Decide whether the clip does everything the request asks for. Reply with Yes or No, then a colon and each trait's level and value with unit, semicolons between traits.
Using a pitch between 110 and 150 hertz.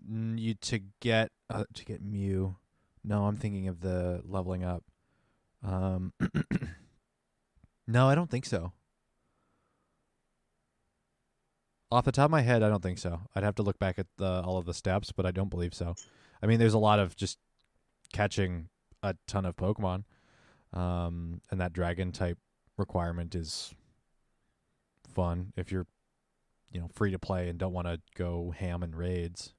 No: very low, 95 Hz